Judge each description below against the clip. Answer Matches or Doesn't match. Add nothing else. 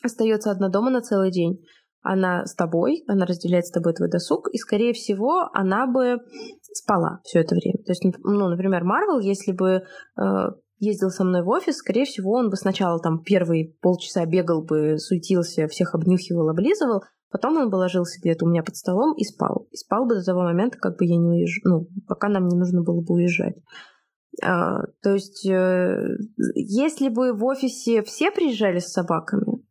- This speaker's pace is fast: Matches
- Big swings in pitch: Doesn't match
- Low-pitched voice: Doesn't match